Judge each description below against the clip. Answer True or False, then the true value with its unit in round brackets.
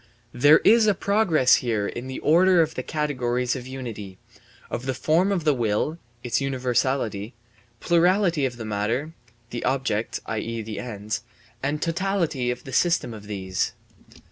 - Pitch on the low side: True (130 Hz)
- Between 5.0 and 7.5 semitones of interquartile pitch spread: True (5.6 semitones)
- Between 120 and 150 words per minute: False (160 wpm)